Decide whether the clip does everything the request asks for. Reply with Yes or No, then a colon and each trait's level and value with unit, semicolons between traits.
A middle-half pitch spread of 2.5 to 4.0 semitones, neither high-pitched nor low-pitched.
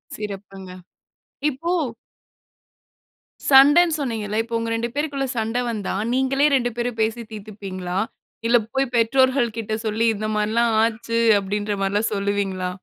No: average, 3.4 semitones; high, 225 Hz